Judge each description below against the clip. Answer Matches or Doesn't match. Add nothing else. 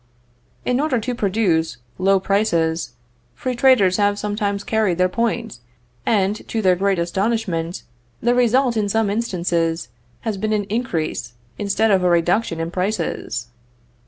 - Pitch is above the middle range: Matches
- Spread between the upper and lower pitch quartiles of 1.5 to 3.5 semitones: Doesn't match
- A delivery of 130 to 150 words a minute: Matches